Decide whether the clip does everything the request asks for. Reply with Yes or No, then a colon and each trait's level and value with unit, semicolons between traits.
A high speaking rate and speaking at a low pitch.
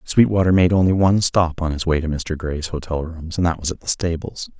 Yes: fast, 250 wpm; very low, 85 Hz